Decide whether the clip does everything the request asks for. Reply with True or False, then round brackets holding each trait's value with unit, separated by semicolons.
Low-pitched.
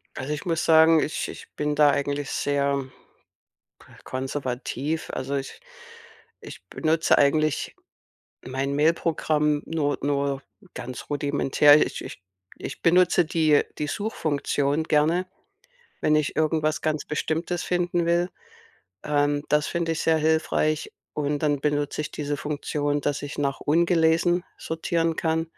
False (150 Hz)